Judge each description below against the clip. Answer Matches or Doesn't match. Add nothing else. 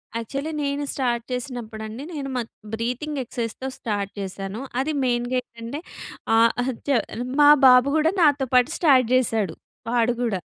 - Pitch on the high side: Matches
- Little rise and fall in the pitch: Doesn't match